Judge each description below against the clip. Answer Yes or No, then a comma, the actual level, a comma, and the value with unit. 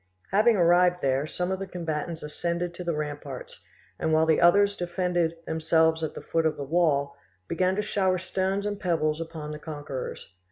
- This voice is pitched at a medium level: Yes, medium, 170 Hz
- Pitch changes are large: No, average, 2.8 semitones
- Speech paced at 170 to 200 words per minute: Yes, average, 185 wpm